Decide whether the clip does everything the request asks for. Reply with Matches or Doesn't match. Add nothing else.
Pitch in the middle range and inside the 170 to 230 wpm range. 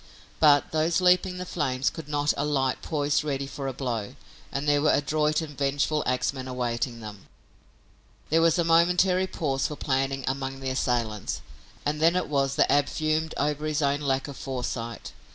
Matches